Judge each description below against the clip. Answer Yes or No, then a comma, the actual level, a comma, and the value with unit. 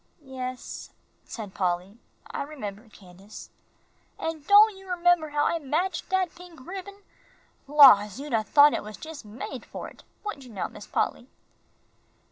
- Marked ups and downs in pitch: Yes, wide, 8.3 semitones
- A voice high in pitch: Yes, very high, 285 Hz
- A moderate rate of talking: Yes, average, 150 wpm